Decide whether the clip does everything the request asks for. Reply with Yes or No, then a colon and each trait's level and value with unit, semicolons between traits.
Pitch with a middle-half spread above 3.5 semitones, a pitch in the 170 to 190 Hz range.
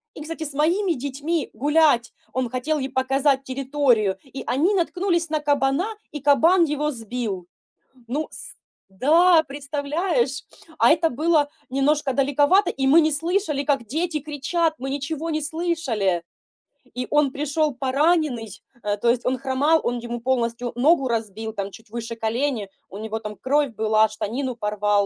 No: average, 4.5 semitones; very high, 275 Hz